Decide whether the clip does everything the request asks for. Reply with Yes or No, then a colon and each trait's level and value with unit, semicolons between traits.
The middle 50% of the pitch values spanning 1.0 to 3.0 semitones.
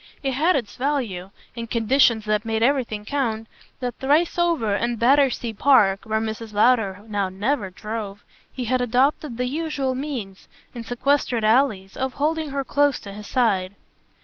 No: average, 4.5 semitones